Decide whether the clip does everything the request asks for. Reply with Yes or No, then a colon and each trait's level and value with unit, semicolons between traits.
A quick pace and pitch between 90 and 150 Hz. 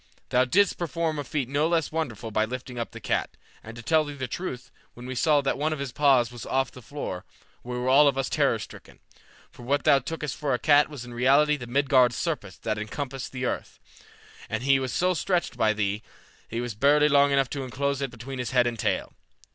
Yes: fast, 235 wpm; low, 135 Hz